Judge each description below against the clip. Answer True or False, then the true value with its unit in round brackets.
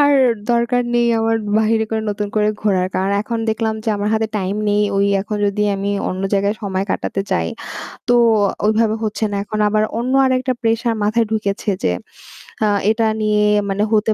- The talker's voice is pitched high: True (215 Hz)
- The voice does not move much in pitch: True (2.0 semitones)